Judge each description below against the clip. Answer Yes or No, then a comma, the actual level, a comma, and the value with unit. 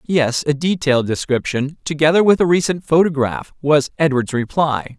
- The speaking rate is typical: Yes, average, 145 wpm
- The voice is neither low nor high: Yes, medium, 150 Hz